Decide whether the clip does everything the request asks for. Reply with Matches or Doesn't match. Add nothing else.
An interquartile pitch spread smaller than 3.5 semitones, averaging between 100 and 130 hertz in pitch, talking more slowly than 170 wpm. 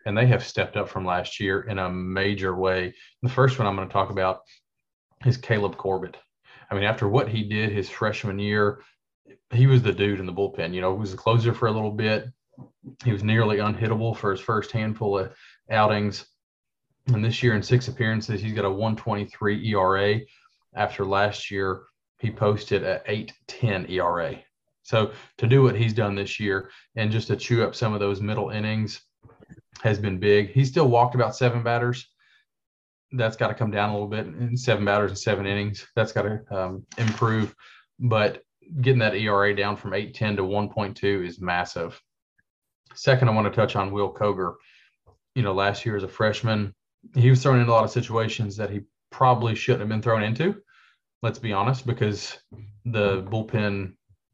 Doesn't match